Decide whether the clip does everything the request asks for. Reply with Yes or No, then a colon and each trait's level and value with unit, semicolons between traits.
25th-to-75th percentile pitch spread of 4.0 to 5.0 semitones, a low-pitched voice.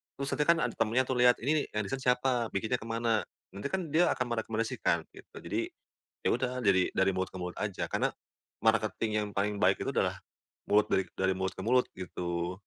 Yes: average, 4.5 semitones; low, 110 Hz